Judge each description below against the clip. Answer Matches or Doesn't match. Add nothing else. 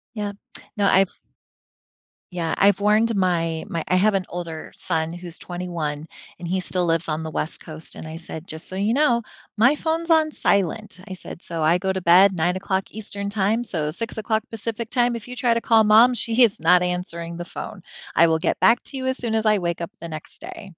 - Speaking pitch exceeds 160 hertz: Matches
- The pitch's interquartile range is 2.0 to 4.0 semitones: Doesn't match